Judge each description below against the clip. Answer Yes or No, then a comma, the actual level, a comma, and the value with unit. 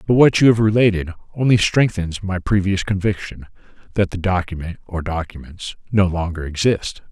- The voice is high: No, very low, 95 Hz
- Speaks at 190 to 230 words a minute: No, average, 150 wpm